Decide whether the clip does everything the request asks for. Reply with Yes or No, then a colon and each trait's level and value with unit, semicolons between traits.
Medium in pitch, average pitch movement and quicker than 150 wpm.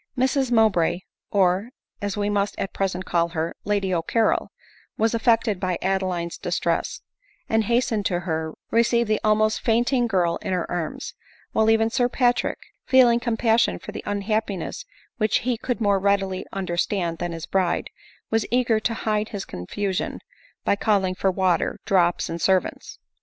No: high, 205 Hz; average, 3.5 semitones; average, 160 wpm